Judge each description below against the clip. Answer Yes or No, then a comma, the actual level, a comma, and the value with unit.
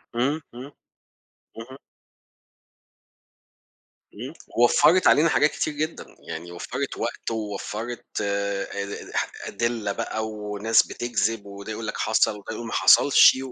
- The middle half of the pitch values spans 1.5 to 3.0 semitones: No, average, 3.9 semitones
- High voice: No, low, 115 Hz